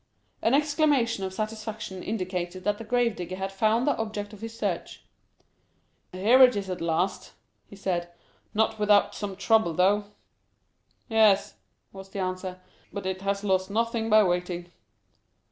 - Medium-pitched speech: No, high, 200 Hz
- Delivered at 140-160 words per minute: Yes, average, 150 wpm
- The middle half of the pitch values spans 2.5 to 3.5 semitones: Yes, average, 3.1 semitones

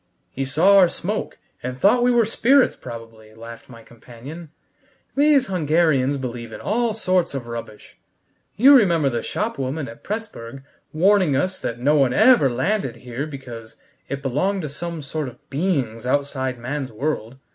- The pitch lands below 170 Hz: Yes, medium, 140 Hz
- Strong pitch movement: Yes, wide, 7.4 semitones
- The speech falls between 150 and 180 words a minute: Yes, average, 155 wpm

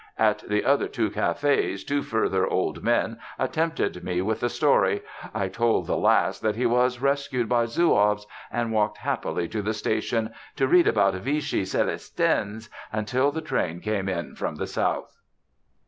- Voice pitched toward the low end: Yes, low, 110 Hz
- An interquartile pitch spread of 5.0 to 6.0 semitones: No, average, 3.8 semitones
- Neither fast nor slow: Yes, average, 160 wpm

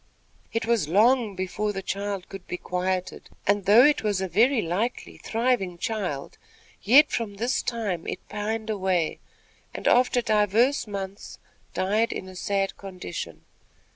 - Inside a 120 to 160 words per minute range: Yes, average, 145 wpm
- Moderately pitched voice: No, high, 205 Hz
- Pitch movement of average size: Yes, average, 3.4 semitones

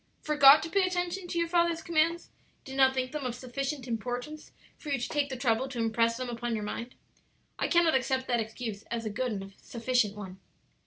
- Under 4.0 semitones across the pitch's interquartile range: No, average, 4.7 semitones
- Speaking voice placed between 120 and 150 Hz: No, very high, 255 Hz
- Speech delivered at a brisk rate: Yes, fast, 210 wpm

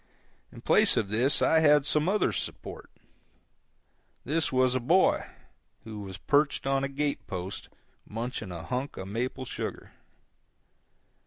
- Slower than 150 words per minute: Yes, average, 140 wpm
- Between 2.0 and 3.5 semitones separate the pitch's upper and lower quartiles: No, average, 5.0 semitones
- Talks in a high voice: No, low, 130 Hz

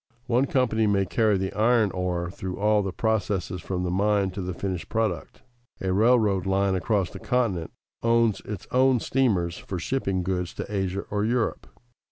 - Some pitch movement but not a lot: Yes, average, 3.3 semitones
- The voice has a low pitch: Yes, low, 100 Hz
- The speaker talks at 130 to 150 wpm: No, average, 175 wpm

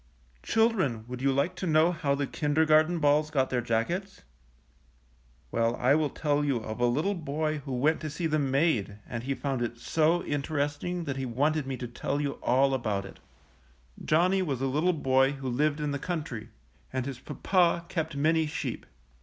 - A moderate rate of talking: Yes, average, 190 wpm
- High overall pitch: No, medium, 145 Hz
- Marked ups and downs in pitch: No, average, 3.3 semitones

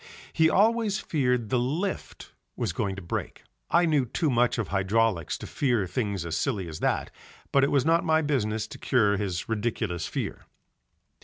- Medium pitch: No, low, 120 Hz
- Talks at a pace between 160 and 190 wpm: Yes, average, 175 wpm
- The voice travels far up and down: Yes, wide, 6.8 semitones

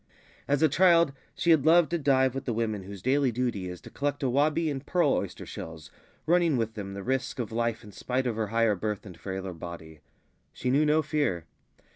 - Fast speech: Yes, fast, 210 wpm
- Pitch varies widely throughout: Yes, wide, 6.1 semitones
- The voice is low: Yes, low, 125 Hz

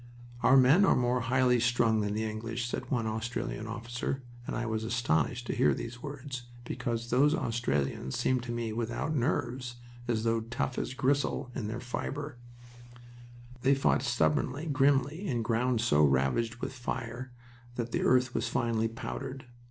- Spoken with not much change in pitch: Yes, narrow, 2.3 semitones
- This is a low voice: Yes, low, 120 Hz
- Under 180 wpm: Yes, average, 160 wpm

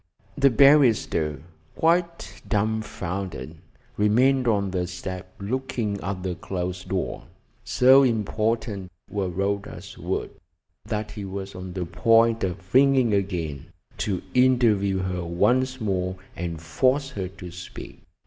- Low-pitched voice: Yes, low, 100 Hz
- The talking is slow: Yes, slow, 120 wpm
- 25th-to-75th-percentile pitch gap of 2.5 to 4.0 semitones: No, average, 4.6 semitones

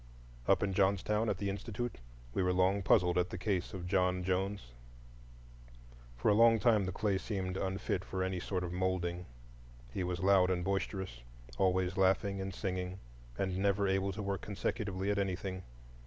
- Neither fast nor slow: Yes, average, 170 wpm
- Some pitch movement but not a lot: No, narrow, 1.5 semitones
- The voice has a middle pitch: No, very low, 95 Hz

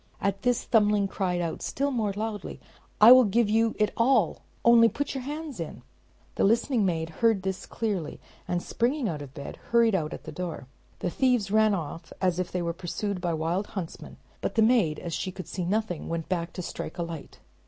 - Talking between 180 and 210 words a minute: Yes, fast, 205 wpm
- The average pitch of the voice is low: No, high, 200 Hz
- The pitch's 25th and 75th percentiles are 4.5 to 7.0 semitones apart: Yes, average, 4.8 semitones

